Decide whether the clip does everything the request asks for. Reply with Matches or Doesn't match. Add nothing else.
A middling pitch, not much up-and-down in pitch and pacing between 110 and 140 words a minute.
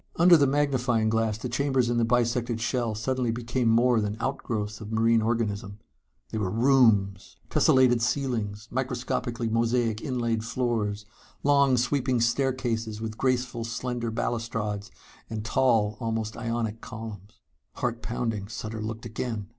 Doesn't match